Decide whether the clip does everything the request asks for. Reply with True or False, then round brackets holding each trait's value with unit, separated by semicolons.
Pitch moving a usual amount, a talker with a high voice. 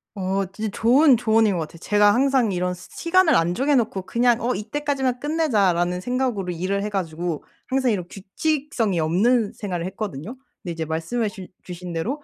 False (5.8 semitones; 210 Hz)